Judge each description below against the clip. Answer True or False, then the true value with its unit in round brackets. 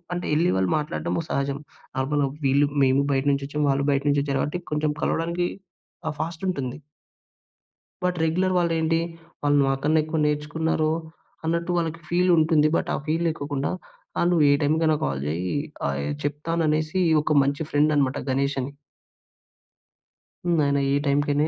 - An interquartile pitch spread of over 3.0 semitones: False (2.7 semitones)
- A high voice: False (150 Hz)